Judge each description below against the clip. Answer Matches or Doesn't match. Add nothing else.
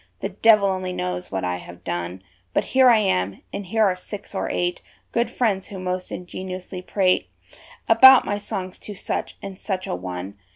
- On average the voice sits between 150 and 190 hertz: Matches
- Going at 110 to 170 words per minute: Doesn't match